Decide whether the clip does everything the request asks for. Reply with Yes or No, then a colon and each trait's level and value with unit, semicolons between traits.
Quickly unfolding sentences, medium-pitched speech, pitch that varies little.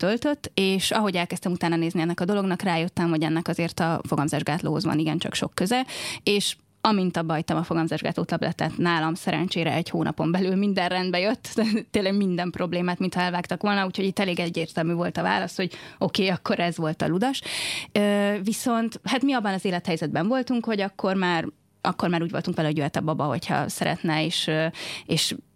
No: fast, 190 wpm; medium, 180 Hz; average, 3.2 semitones